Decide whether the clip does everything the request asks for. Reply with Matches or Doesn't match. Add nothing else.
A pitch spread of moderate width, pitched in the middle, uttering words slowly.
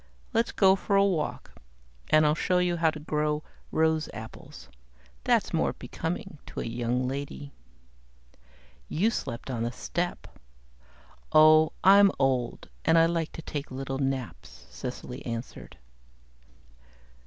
Matches